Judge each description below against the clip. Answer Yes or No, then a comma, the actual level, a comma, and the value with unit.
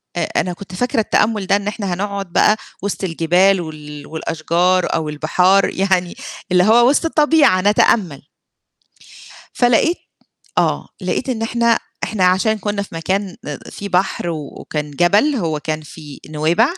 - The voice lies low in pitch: No, medium, 185 Hz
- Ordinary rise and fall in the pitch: Yes, average, 4.4 semitones